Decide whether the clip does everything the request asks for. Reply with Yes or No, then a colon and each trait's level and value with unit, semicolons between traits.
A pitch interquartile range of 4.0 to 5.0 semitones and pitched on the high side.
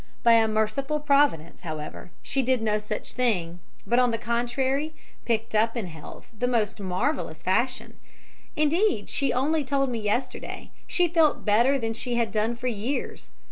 Yes: average, 4.3 semitones; high, 235 Hz